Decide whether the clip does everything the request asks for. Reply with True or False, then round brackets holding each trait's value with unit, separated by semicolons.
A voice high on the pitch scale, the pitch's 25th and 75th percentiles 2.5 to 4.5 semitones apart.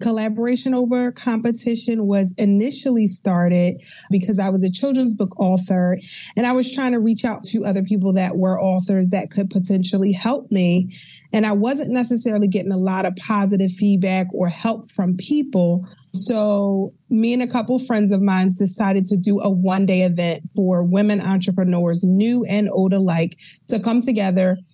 True (200 Hz; 3.4 semitones)